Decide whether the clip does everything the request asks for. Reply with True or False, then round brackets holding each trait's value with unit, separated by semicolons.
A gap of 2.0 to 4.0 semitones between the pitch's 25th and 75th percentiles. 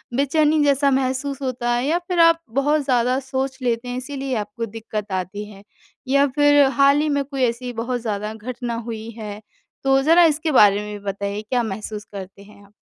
False (4.6 semitones)